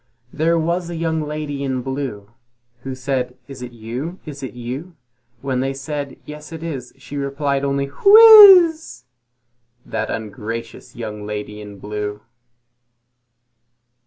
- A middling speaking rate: No, slow, 130 wpm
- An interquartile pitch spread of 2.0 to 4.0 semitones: No, average, 4.5 semitones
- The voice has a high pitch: No, low, 135 Hz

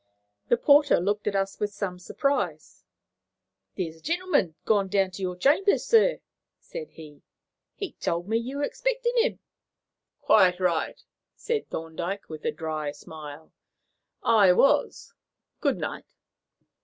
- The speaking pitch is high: Yes, high, 195 Hz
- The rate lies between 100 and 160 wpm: Yes, average, 140 wpm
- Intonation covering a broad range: Yes, wide, 8.9 semitones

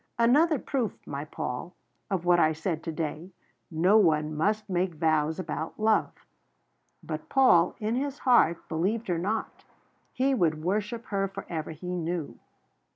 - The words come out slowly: No, average, 150 wpm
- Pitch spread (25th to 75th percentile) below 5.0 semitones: No, average, 5.3 semitones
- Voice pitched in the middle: Yes, medium, 180 Hz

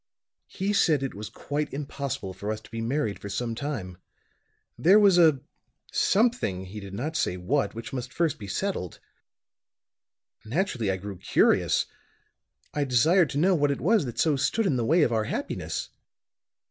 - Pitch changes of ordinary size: No, wide, 7.1 semitones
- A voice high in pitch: No, low, 135 Hz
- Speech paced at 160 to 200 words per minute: Yes, average, 170 wpm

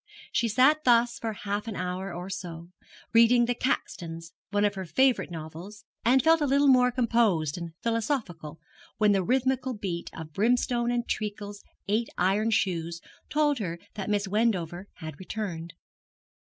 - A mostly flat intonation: No, average, 5.3 semitones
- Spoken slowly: No, average, 155 wpm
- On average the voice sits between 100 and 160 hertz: No, high, 210 Hz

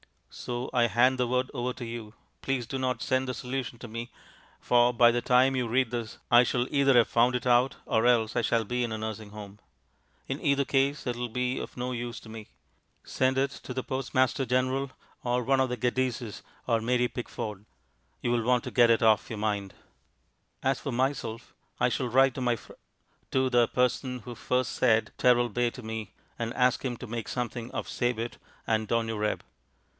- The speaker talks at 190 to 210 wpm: Yes, average, 200 wpm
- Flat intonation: Yes, narrow, 1.8 semitones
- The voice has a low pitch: Yes, low, 120 Hz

